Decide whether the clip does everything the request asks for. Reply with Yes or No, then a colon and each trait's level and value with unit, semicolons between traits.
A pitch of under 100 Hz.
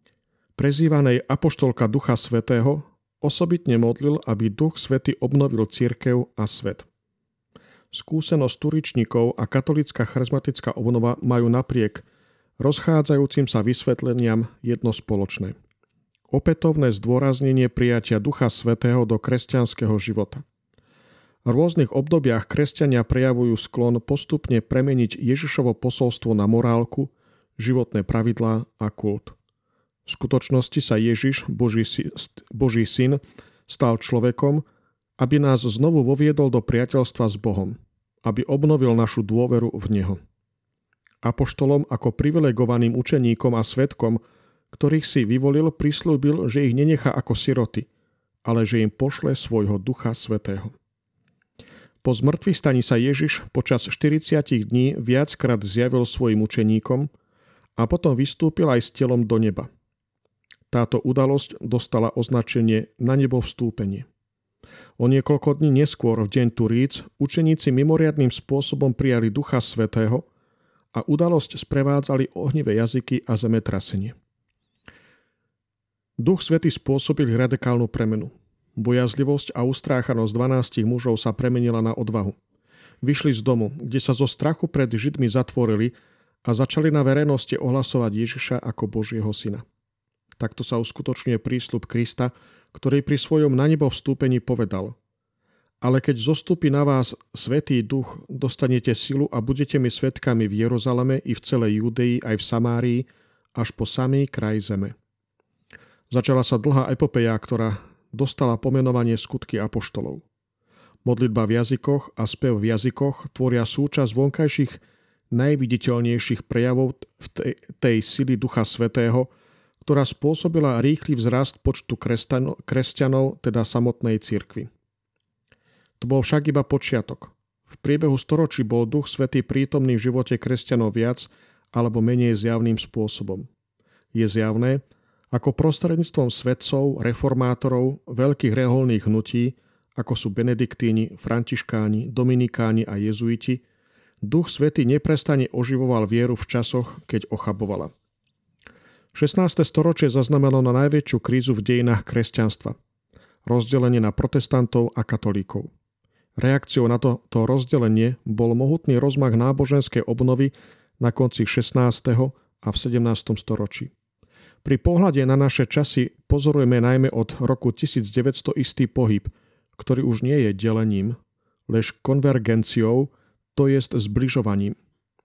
No: low, 125 Hz